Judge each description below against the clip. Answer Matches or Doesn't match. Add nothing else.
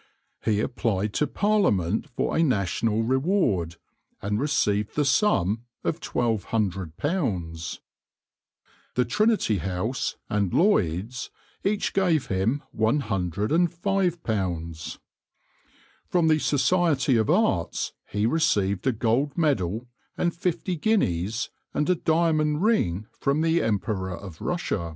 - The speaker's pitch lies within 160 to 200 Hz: Doesn't match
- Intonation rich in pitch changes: Matches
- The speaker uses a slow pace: Matches